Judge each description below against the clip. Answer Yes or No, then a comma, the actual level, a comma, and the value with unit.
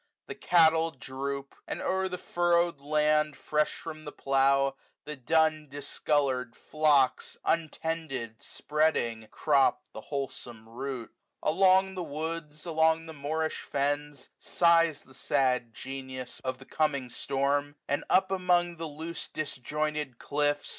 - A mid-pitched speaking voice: Yes, medium, 150 Hz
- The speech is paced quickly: No, slow, 135 wpm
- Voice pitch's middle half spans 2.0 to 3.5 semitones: Yes, average, 2.9 semitones